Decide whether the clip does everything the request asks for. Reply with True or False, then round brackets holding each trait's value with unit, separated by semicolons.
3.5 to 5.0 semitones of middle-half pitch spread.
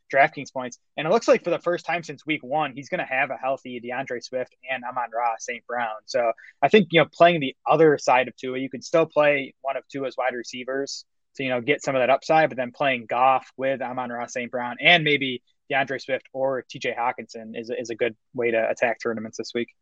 False (3.1 semitones)